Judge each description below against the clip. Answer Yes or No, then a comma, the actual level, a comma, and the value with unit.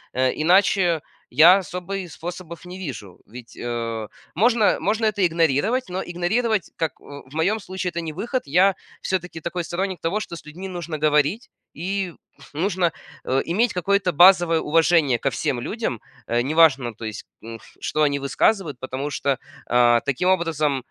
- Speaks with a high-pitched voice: No, medium, 170 Hz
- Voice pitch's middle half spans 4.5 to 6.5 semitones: Yes, average, 5.0 semitones